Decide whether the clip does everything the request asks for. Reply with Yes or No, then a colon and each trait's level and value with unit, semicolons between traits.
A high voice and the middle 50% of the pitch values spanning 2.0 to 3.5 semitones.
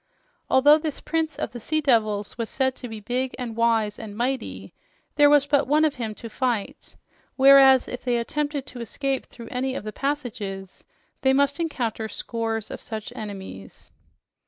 No: very high, 250 Hz; average, 3.9 semitones